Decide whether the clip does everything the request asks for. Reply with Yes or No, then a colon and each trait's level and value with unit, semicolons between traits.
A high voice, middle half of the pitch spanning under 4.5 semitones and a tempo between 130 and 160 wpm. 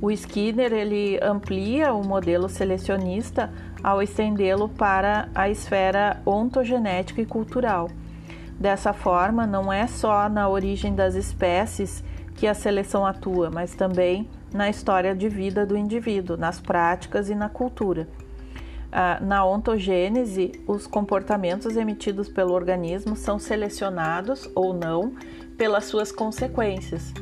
No: high, 195 Hz; average, 2.7 semitones; slow, 120 wpm